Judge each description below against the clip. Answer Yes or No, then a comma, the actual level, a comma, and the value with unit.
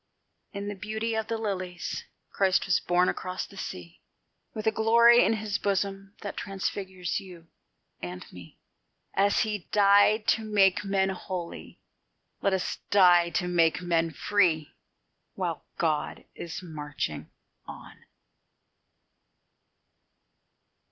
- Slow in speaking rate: Yes, slow, 120 wpm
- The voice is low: No, high, 195 Hz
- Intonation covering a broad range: No, average, 2.8 semitones